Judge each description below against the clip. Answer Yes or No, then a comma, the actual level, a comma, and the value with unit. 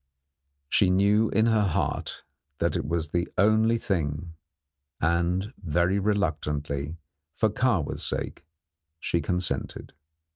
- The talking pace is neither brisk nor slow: No, slow, 110 wpm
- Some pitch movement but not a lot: Yes, average, 4.1 semitones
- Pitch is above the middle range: No, very low, 90 Hz